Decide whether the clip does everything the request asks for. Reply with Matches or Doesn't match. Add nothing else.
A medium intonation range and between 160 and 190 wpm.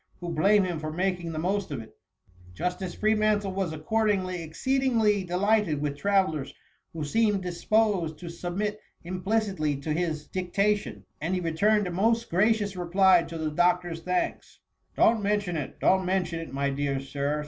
Matches